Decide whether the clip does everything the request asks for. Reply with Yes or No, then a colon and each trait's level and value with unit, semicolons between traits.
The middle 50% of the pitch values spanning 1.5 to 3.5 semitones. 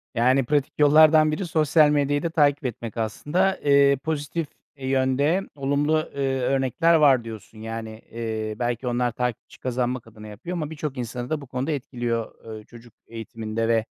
No: average, 4.2 semitones